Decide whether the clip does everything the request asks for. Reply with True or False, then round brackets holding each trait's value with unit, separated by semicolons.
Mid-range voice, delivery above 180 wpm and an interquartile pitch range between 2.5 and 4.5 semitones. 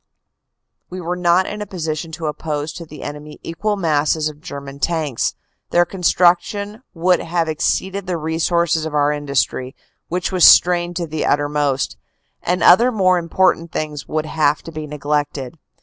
False (160 Hz; 165 wpm; 3.0 semitones)